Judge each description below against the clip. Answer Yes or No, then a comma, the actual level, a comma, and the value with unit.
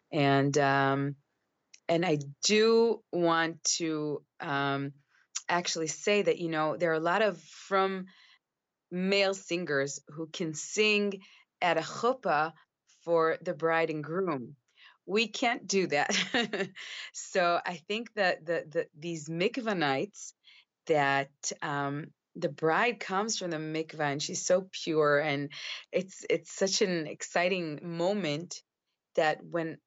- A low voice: No, medium, 170 Hz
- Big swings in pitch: No, average, 4.1 semitones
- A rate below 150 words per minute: Yes, slow, 135 wpm